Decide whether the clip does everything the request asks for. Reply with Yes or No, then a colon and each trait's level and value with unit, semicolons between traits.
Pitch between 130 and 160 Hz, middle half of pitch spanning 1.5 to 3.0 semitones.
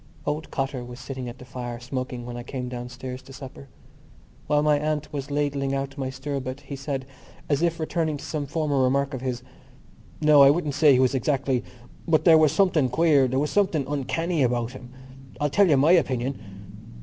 Yes: medium, 140 Hz; average, 2.7 semitones